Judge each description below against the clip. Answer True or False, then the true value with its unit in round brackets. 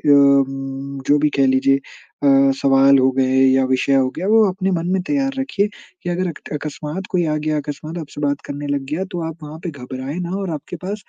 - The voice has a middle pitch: True (145 Hz)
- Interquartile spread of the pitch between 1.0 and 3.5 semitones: False (4.2 semitones)